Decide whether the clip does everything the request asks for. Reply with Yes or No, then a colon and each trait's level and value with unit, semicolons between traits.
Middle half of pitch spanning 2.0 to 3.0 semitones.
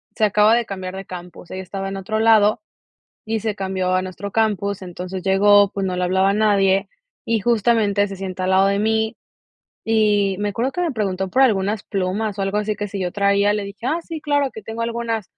Yes: narrow, 2.4 semitones